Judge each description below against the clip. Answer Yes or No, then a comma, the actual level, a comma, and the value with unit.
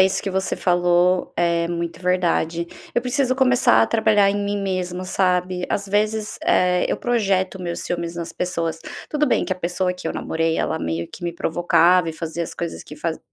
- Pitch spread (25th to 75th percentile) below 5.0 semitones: Yes, narrow, 2.5 semitones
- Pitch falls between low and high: Yes, medium, 180 Hz